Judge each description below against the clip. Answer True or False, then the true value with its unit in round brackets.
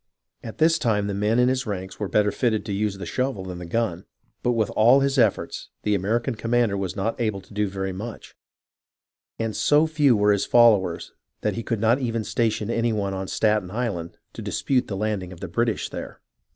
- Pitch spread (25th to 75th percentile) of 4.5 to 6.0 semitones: False (3.2 semitones)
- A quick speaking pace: True (210 wpm)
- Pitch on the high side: False (110 Hz)